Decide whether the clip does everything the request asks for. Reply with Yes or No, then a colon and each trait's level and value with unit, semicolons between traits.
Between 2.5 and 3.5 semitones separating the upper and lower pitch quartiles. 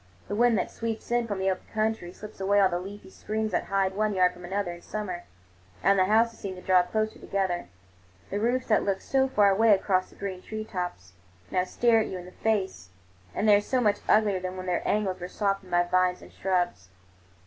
Yes: average, 2.8 semitones